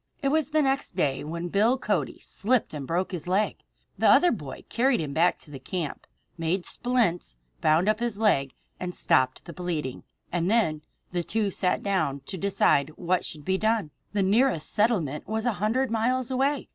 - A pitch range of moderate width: No, wide, 6.3 semitones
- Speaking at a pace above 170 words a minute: Yes, average, 185 wpm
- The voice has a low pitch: No, high, 190 Hz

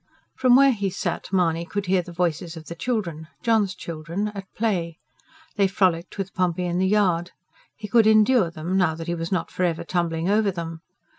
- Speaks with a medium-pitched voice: Yes, medium, 180 Hz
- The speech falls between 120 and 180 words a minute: No, average, 200 wpm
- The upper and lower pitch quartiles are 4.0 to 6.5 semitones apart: No, average, 3.4 semitones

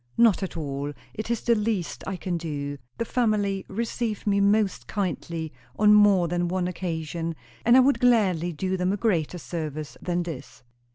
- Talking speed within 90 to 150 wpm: No, average, 175 wpm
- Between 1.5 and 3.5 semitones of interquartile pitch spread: No, average, 4.3 semitones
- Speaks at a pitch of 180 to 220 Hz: Yes, medium, 185 Hz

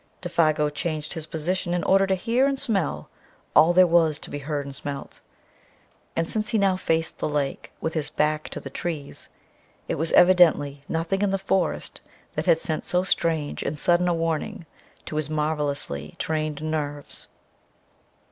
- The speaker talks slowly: No, average, 170 wpm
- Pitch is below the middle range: No, medium, 160 Hz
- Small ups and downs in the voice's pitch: No, average, 3.0 semitones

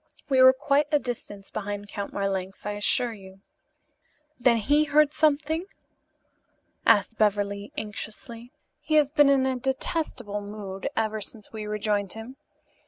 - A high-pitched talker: Yes, high, 225 Hz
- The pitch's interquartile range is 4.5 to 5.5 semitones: Yes, average, 5.0 semitones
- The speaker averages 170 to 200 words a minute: No, average, 140 wpm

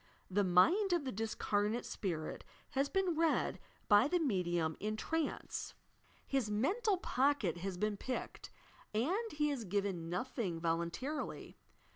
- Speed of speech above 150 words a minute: No, slow, 135 wpm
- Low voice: No, high, 220 Hz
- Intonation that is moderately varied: No, wide, 8.3 semitones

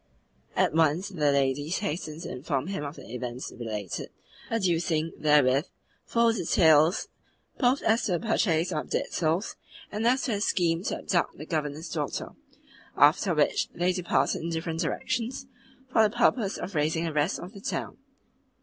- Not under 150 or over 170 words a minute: Yes, average, 165 wpm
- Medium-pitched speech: Yes, medium, 165 Hz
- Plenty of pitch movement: No, average, 4.9 semitones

